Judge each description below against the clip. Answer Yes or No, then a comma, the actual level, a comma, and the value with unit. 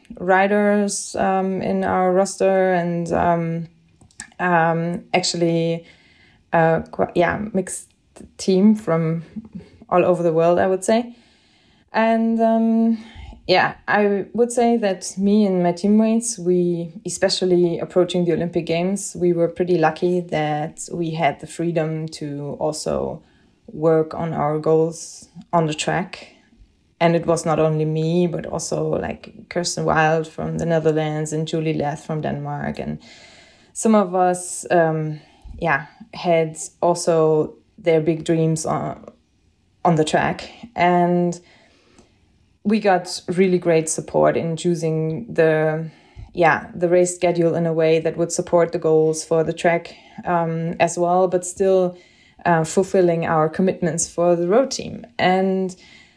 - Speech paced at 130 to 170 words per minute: Yes, slow, 135 wpm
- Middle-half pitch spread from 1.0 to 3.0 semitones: Yes, average, 2.7 semitones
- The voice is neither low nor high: Yes, medium, 170 Hz